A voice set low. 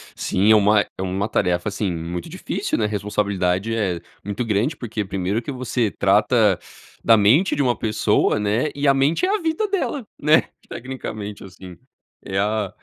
Yes: low, 105 Hz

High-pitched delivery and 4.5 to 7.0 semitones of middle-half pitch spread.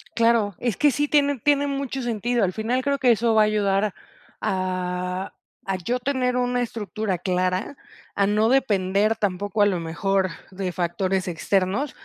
Yes: high, 210 Hz; average, 4.9 semitones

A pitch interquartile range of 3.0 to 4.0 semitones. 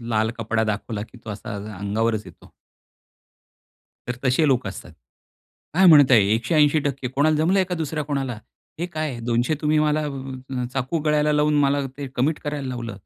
No: average, 4.9 semitones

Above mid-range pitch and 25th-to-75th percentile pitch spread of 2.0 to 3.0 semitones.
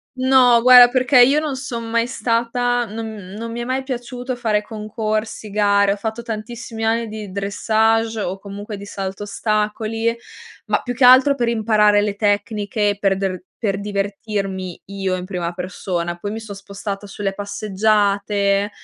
Yes: high, 215 Hz; narrow, 2.6 semitones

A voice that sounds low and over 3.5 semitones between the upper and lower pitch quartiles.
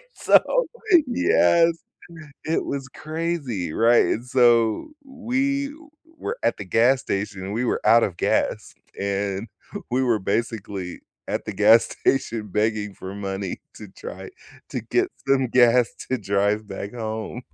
Yes: low, 115 Hz; average, 4.8 semitones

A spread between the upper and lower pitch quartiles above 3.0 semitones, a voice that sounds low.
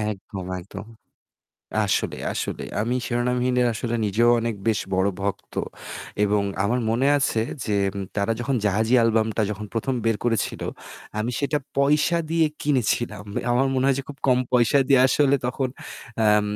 Yes: average, 3.7 semitones; low, 115 Hz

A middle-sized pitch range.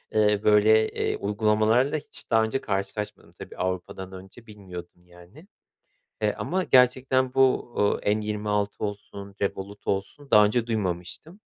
Yes: average, 3.2 semitones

